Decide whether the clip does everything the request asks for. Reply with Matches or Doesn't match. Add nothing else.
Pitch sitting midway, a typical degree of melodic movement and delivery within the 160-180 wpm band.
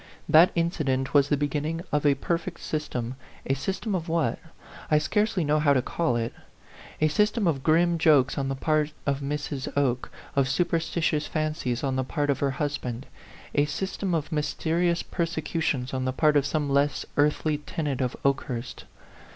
Matches